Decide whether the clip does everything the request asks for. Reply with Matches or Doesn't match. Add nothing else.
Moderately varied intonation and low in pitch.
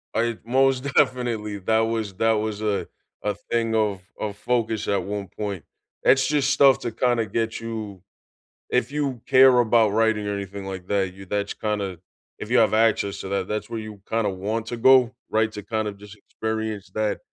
Doesn't match